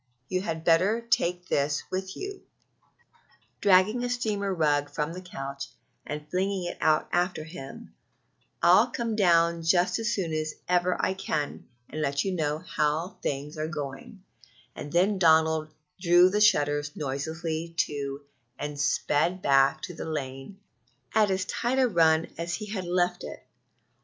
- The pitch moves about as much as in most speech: Yes, average, 4.0 semitones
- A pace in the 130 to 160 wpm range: Yes, average, 155 wpm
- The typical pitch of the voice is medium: Yes, medium, 170 Hz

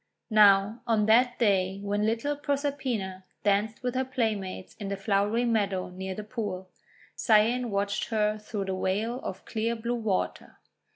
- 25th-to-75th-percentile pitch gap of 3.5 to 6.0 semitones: No, average, 3.0 semitones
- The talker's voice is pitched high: Yes, high, 215 Hz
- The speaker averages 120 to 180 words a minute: Yes, average, 155 wpm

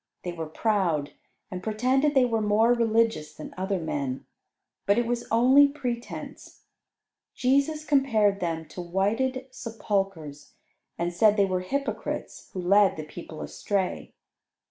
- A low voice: No, high, 205 Hz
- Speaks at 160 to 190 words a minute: No, slow, 135 wpm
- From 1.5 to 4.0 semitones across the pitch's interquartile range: No, wide, 5.6 semitones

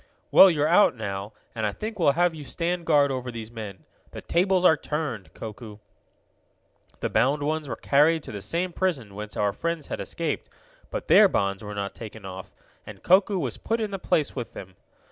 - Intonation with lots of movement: Yes, wide, 8.0 semitones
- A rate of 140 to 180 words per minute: No, average, 200 wpm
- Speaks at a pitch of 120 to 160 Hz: Yes, medium, 140 Hz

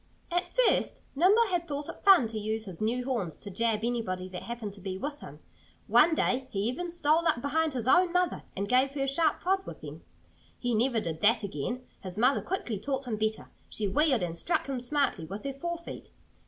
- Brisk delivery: Yes, fast, 220 wpm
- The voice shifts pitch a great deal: Yes, wide, 6.1 semitones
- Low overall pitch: No, very high, 250 Hz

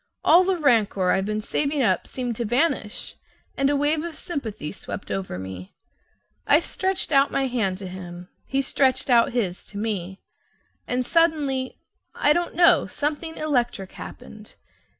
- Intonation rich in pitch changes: Yes, wide, 6.8 semitones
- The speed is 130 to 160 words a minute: Yes, average, 155 wpm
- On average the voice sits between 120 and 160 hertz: No, very high, 250 Hz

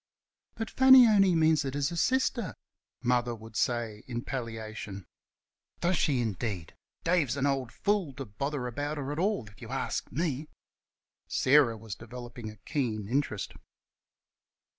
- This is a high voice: No, low, 130 Hz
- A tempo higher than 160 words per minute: No, average, 145 wpm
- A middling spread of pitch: No, wide, 5.7 semitones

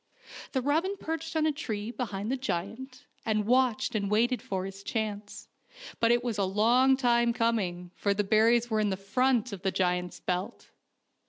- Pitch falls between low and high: No, high, 225 Hz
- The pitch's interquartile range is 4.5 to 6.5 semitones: No, average, 4.1 semitones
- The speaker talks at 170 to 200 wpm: Yes, average, 175 wpm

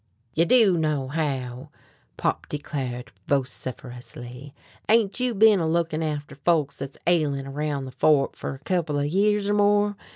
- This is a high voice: No, medium, 150 Hz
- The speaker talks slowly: No, average, 155 wpm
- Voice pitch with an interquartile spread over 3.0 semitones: Yes, average, 5.1 semitones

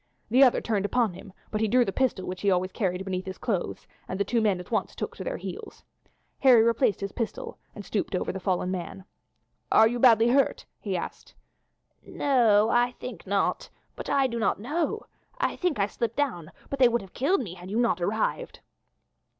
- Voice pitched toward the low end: No, high, 220 Hz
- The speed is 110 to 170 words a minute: No, fast, 205 wpm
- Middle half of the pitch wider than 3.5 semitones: Yes, average, 4.6 semitones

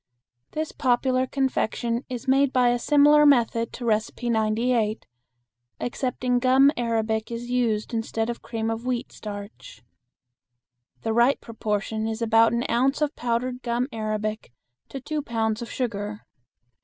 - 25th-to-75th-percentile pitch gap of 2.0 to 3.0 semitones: Yes, narrow, 2.4 semitones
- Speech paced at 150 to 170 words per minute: No, average, 140 wpm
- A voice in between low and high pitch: No, high, 235 Hz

